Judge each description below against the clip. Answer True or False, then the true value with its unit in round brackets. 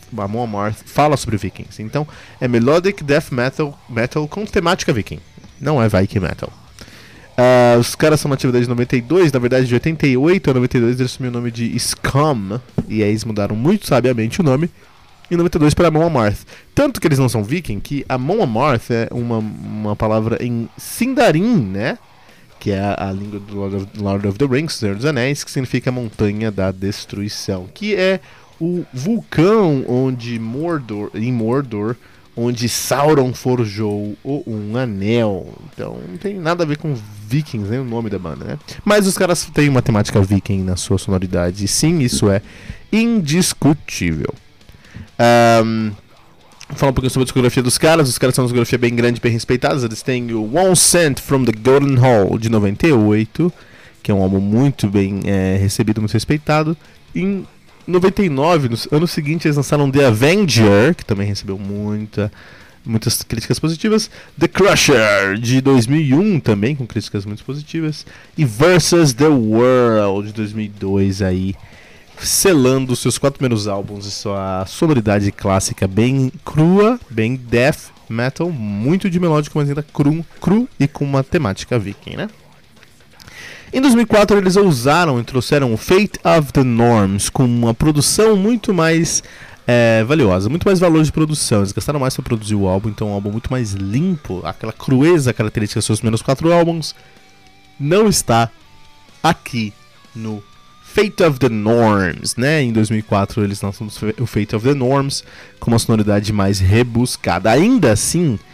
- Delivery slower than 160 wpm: False (165 wpm)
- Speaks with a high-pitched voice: False (120 Hz)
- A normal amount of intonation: False (6.0 semitones)